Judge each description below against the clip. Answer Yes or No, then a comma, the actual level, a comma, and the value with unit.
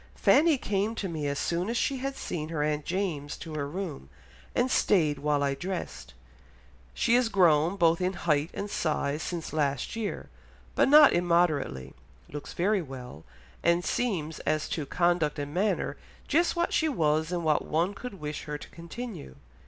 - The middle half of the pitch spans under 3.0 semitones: No, average, 5.1 semitones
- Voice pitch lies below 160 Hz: No, medium, 170 Hz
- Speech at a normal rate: Yes, average, 175 wpm